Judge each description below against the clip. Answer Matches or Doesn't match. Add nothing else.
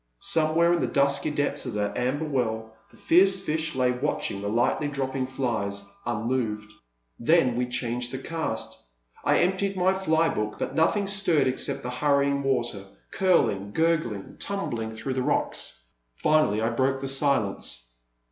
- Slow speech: Doesn't match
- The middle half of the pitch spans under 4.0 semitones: Doesn't match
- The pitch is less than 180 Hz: Matches